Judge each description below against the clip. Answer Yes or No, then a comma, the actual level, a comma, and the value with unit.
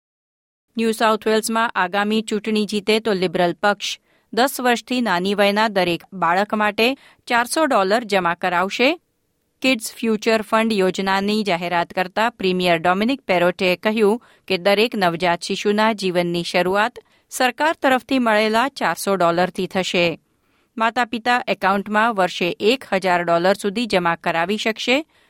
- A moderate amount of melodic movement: Yes, average, 3.6 semitones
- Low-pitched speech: No, high, 210 Hz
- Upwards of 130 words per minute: No, average, 120 wpm